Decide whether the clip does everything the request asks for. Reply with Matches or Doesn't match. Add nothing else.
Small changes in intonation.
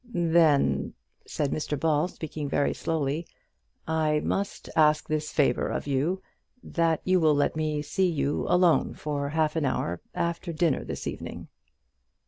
Matches